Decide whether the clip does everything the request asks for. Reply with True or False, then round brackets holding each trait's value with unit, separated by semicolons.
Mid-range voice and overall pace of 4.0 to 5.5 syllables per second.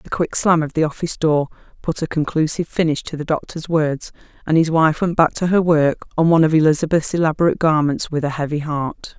False (155 Hz; 5.9 syllables/s)